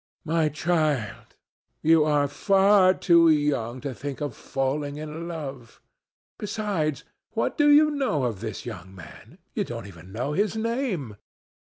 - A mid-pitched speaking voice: Yes, medium, 150 Hz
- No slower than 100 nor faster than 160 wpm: Yes, average, 145 wpm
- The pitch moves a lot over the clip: Yes, wide, 6.1 semitones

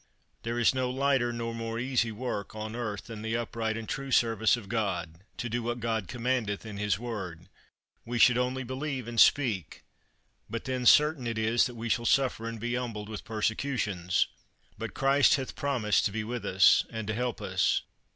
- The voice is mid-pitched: No, low, 115 Hz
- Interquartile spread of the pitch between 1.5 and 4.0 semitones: Yes, narrow, 2.5 semitones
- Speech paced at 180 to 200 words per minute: Yes, average, 190 wpm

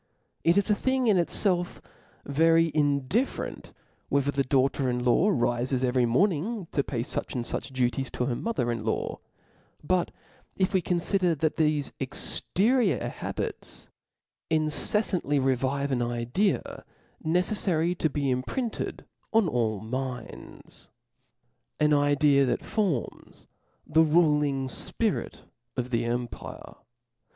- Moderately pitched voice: Yes, medium, 145 Hz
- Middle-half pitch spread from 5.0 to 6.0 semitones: Yes, wide, 5.6 semitones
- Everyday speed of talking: No, slow, 130 wpm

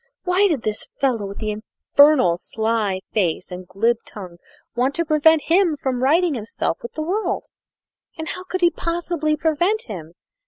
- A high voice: Yes, very high, 275 Hz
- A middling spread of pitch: No, wide, 7.8 semitones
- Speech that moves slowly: No, average, 165 wpm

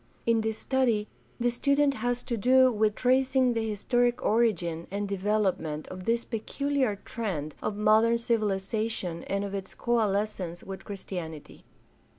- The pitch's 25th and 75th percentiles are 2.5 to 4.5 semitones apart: Yes, average, 3.5 semitones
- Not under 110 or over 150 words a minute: Yes, average, 140 wpm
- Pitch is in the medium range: No, high, 215 Hz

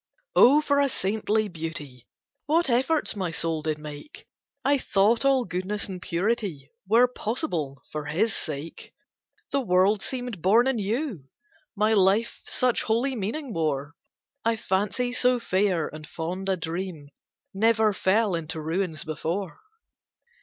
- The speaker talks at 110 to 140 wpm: Yes, slow, 135 wpm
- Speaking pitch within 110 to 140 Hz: No, high, 195 Hz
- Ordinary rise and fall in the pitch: No, wide, 6.3 semitones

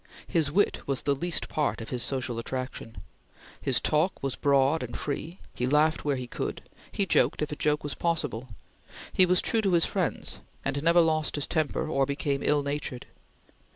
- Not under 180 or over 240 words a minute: Yes, average, 190 wpm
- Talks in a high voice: No, medium, 145 Hz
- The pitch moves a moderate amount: Yes, average, 3.1 semitones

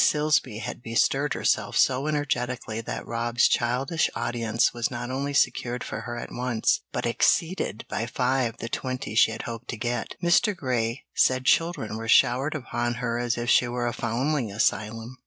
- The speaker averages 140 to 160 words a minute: No, average, 175 wpm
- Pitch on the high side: No, low, 120 Hz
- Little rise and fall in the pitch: Yes, narrow, 2.3 semitones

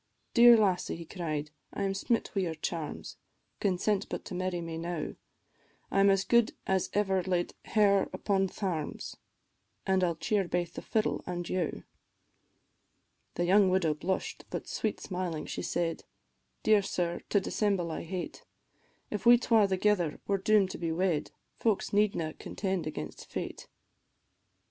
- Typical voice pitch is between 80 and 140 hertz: No, medium, 185 Hz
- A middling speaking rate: Yes, average, 155 wpm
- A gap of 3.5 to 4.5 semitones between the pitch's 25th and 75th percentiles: No, average, 2.9 semitones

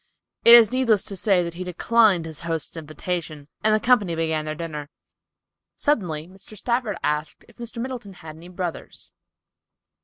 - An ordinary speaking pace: Yes, average, 160 wpm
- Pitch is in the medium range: Yes, medium, 180 Hz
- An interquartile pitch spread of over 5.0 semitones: Yes, wide, 5.4 semitones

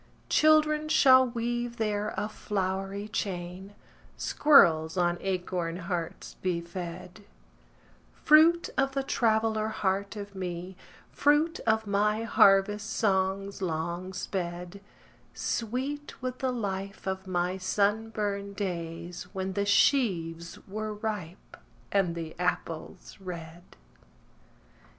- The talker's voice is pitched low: No, high, 200 Hz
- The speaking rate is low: Yes, slow, 105 wpm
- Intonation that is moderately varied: Yes, average, 3.6 semitones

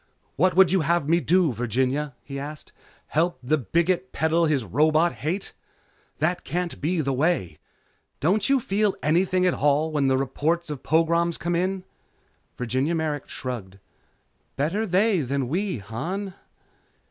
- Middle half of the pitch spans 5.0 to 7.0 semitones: No, average, 4.5 semitones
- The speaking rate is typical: Yes, average, 145 wpm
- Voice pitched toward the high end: No, medium, 160 Hz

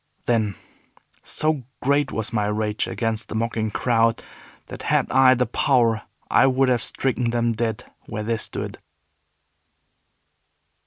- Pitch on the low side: Yes, low, 115 Hz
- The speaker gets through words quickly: No, slow, 135 wpm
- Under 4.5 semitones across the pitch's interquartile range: Yes, narrow, 2.6 semitones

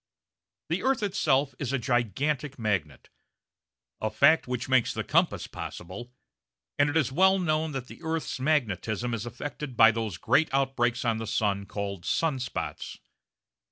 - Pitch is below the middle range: Yes, low, 125 Hz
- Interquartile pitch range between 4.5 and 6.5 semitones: Yes, average, 5.2 semitones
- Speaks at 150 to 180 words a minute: Yes, average, 155 wpm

